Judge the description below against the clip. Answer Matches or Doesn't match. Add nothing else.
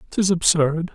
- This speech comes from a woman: Doesn't match